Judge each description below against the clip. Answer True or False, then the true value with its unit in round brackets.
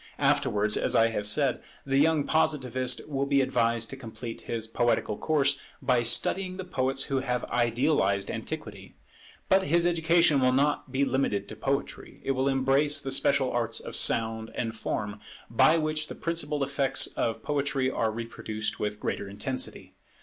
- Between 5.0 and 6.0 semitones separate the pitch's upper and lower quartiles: False (4.0 semitones)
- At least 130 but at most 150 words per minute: False (165 wpm)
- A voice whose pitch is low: True (130 Hz)